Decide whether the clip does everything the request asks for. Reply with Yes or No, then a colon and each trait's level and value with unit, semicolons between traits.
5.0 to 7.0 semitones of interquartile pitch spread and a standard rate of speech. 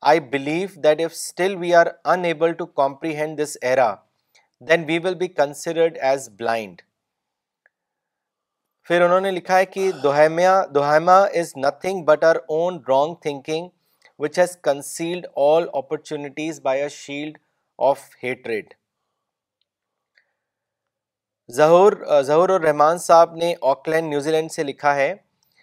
No: average, 3.2 semitones; average, 130 wpm